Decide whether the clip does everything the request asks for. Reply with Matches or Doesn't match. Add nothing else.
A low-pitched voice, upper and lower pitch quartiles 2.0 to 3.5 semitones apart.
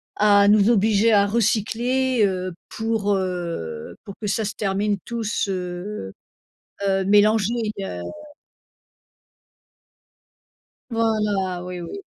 Doesn't match